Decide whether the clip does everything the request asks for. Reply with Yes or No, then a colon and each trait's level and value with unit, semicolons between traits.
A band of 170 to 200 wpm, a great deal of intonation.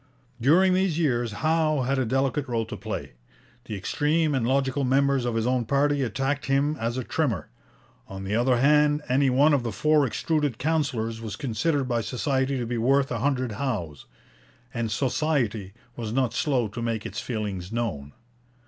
No: average, 175 wpm; average, 4.0 semitones